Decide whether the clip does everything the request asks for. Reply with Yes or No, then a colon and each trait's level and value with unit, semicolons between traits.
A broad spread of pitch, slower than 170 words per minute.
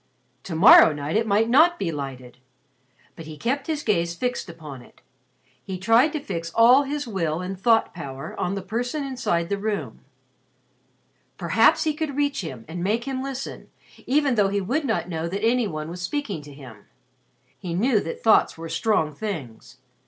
No: wide, 7.4 semitones; average, 180 wpm